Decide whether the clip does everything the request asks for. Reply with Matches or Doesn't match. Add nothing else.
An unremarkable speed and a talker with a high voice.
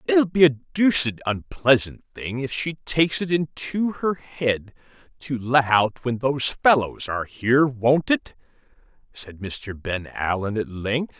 Doesn't match